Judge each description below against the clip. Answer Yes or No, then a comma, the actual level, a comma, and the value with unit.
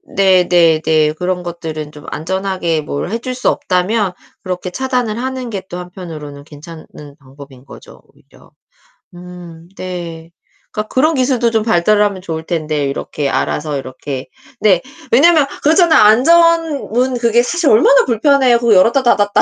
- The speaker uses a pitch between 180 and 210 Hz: Yes, medium, 185 Hz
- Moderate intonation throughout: No, wide, 7.1 semitones